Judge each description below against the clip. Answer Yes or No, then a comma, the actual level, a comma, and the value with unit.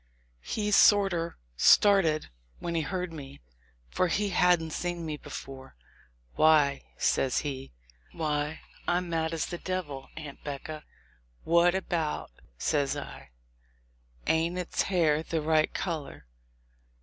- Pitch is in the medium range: Yes, medium, 160 Hz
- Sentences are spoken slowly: Yes, slow, 120 wpm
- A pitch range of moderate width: Yes, average, 3.1 semitones